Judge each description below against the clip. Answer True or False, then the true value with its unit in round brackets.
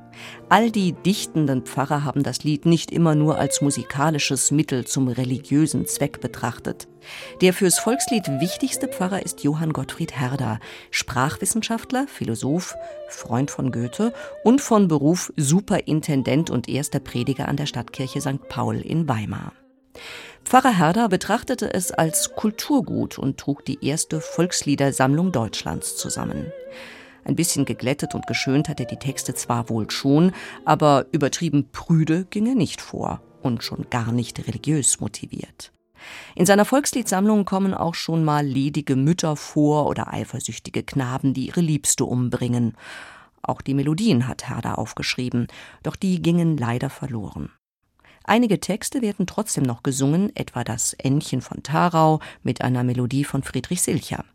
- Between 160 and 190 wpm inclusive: False (140 wpm)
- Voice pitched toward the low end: False (150 Hz)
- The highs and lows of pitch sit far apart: True (5.9 semitones)